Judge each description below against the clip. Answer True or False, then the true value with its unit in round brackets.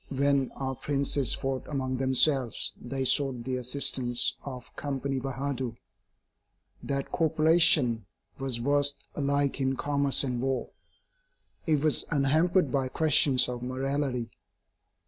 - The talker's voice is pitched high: False (135 Hz)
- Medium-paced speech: False (115 wpm)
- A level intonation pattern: True (1.8 semitones)